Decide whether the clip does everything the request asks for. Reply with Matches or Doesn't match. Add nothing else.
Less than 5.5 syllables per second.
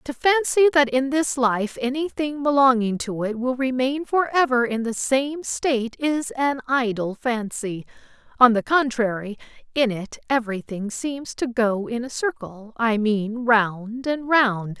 Matches